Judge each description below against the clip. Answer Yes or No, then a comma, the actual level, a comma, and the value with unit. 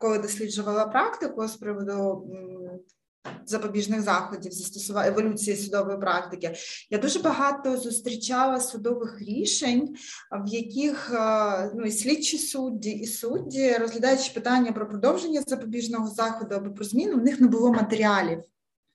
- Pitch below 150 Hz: No, high, 225 Hz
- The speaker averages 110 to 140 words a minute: Yes, average, 125 wpm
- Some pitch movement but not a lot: Yes, average, 3.9 semitones